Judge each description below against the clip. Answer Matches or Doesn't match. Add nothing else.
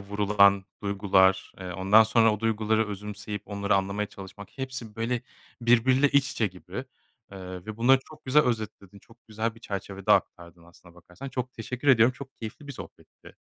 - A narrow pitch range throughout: Doesn't match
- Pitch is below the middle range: Matches